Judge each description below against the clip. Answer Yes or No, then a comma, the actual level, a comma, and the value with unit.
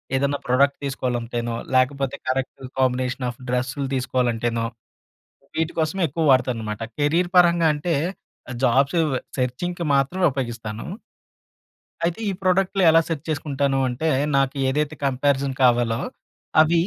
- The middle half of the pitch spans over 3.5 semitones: Yes, average, 4.0 semitones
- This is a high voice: No, low, 135 Hz